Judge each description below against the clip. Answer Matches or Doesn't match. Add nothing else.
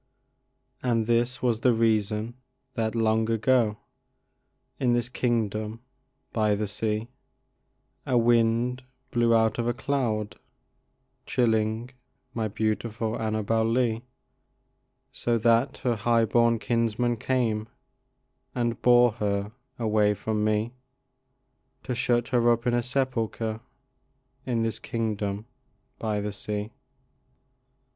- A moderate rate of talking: Doesn't match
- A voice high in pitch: Doesn't match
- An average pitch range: Doesn't match